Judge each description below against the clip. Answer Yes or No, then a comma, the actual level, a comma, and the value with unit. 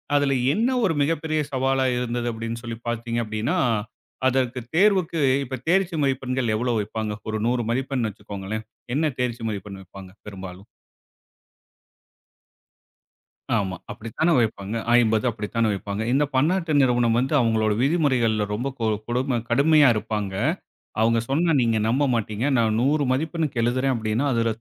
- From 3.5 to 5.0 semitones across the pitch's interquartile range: Yes, average, 4.0 semitones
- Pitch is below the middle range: Yes, low, 120 Hz